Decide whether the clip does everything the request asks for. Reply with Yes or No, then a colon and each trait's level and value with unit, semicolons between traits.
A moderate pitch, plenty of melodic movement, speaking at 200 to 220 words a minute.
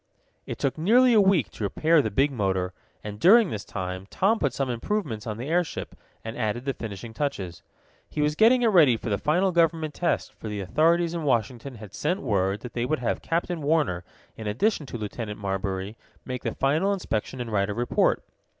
No: low, 130 Hz; wide, 7.8 semitones; fast, 205 wpm